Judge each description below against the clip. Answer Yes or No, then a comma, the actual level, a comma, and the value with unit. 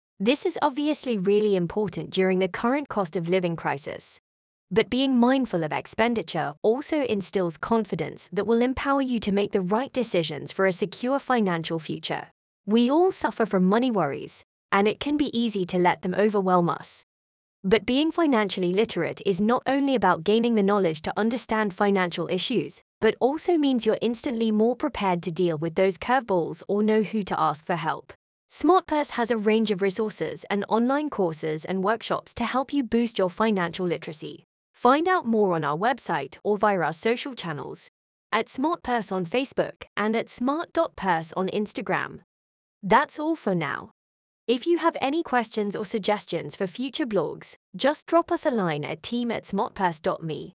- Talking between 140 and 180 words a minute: Yes, average, 170 wpm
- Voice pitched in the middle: No, high, 215 Hz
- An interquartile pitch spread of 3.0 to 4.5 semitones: No, average, 5.1 semitones